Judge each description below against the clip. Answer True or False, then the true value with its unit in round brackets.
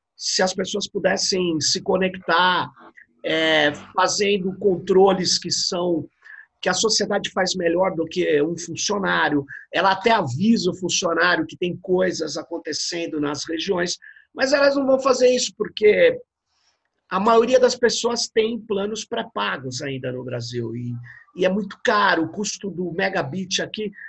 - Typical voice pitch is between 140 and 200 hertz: True (185 Hz)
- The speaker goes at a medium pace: True (145 wpm)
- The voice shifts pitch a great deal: False (4.3 semitones)